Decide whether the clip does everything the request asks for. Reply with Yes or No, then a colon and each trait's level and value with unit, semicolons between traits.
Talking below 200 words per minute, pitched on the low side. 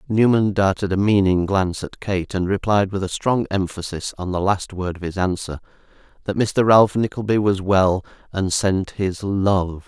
Yes: average, 180 wpm; very low, 95 Hz